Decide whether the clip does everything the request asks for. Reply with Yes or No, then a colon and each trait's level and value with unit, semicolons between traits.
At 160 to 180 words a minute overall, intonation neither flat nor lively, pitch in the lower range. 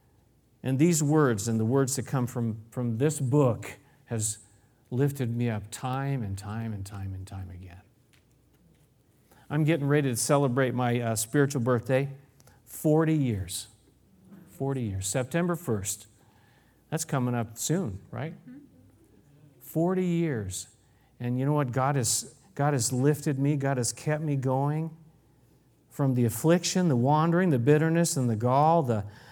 No: average, 145 wpm; average, 4.5 semitones; low, 130 Hz